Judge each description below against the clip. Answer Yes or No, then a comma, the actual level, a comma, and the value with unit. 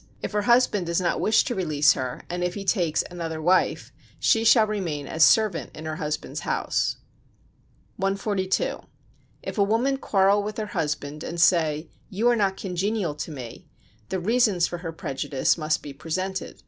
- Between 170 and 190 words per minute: Yes, average, 175 wpm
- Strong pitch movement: No, average, 4.7 semitones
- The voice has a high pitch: No, medium, 180 Hz